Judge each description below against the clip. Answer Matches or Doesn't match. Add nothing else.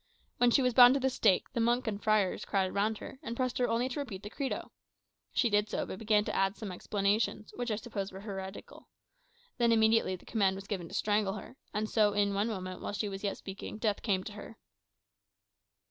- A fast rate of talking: Matches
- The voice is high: Matches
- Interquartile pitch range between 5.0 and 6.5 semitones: Doesn't match